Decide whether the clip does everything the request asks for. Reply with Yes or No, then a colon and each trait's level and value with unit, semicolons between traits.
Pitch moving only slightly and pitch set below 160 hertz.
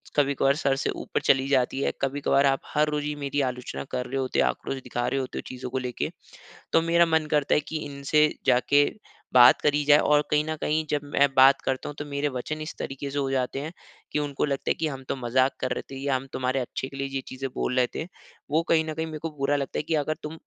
Yes: narrow, 2.1 semitones; medium, 140 Hz